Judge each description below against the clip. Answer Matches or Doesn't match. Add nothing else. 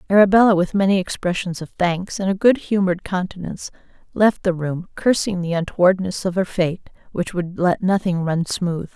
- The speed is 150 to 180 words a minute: Matches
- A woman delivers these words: Matches